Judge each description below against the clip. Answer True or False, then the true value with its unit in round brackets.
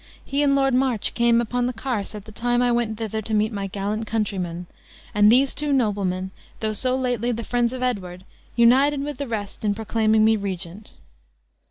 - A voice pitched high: True (225 Hz)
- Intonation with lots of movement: False (3.1 semitones)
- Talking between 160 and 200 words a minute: True (195 wpm)